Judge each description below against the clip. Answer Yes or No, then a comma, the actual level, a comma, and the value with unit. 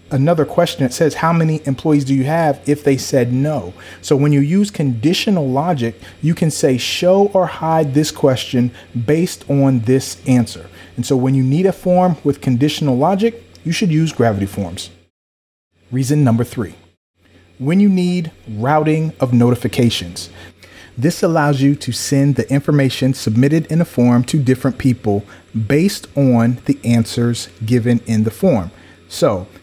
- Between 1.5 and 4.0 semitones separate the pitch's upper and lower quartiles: No, average, 5.1 semitones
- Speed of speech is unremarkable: Yes, average, 160 wpm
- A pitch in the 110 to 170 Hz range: Yes, low, 135 Hz